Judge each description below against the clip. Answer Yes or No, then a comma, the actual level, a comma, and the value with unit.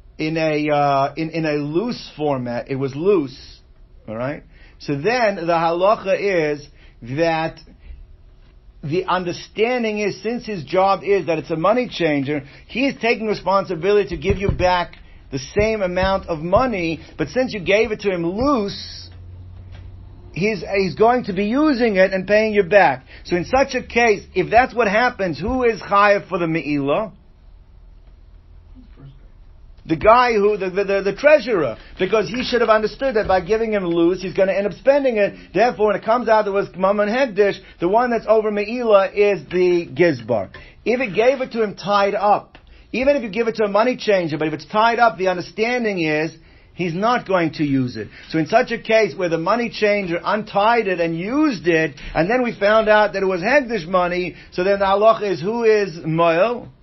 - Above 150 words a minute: Yes, average, 190 wpm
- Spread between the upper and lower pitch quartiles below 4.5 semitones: No, average, 5.0 semitones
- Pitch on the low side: No, high, 195 Hz